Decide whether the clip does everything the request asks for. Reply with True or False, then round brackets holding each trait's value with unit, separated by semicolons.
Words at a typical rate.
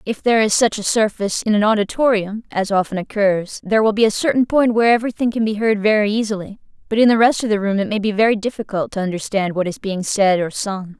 False (245 wpm)